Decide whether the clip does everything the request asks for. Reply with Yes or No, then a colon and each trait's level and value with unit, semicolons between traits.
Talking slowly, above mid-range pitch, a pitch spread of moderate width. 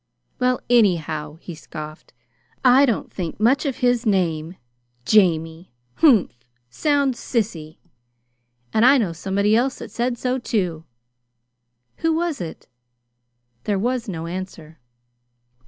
No: slow, 120 wpm; high, 205 Hz; wide, 7.2 semitones